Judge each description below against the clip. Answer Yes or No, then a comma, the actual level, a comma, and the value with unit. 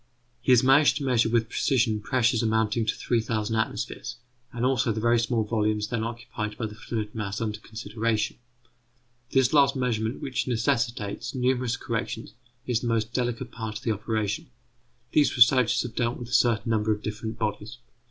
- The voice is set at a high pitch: No, low, 115 Hz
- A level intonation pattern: Yes, narrow, 2.1 semitones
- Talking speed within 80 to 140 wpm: No, average, 170 wpm